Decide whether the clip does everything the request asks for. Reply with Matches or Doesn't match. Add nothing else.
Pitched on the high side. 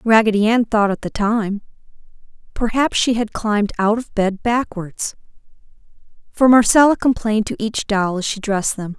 Matches